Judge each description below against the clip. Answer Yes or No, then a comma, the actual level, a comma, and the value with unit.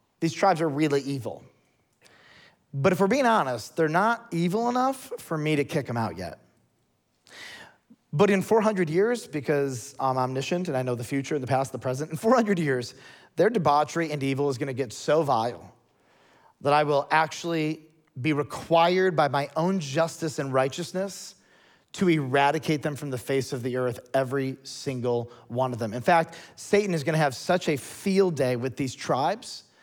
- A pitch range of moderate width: Yes, average, 4.3 semitones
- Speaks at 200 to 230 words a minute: No, average, 180 wpm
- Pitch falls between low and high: Yes, medium, 150 Hz